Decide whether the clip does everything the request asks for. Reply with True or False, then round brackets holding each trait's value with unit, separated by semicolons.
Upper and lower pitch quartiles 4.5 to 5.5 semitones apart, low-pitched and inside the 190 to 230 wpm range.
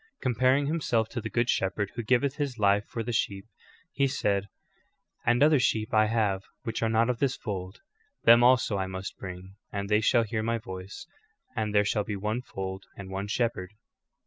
False (3.4 semitones; 110 Hz; 200 wpm)